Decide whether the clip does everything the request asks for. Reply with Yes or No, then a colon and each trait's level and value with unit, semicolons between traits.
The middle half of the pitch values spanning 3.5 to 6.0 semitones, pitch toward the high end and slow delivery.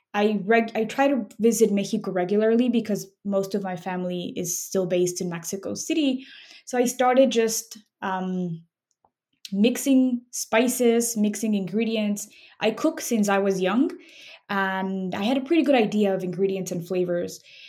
No: average, 4.3 semitones; high, 215 Hz; average, 155 wpm